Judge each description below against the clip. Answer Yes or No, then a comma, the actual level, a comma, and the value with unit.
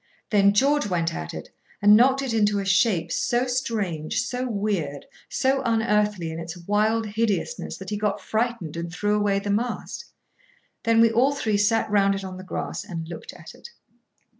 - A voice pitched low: No, high, 210 Hz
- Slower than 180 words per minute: No, average, 185 wpm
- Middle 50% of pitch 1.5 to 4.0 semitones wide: Yes, average, 3.4 semitones